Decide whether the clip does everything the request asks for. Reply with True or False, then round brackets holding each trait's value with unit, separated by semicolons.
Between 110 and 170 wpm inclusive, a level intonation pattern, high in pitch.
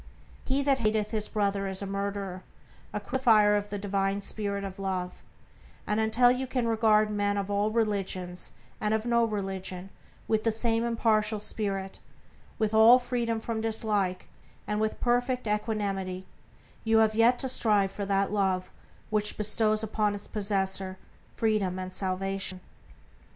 True (150 wpm; 2.3 semitones; 210 Hz)